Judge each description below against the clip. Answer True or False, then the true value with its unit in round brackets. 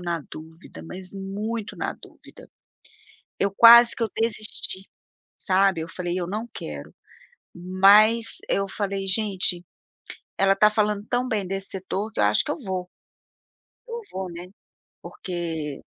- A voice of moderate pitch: False (195 Hz)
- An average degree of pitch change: True (3.0 semitones)